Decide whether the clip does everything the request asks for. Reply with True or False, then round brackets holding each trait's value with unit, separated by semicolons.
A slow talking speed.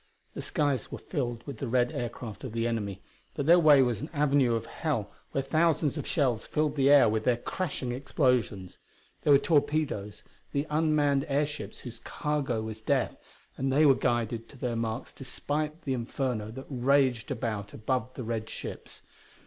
False (175 wpm)